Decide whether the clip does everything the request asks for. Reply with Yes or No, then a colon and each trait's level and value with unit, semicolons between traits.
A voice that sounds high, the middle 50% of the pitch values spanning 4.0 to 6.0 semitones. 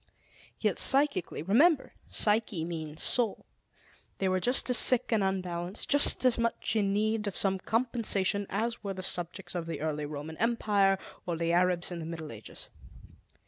Yes: high, 195 Hz; average, 4.7 semitones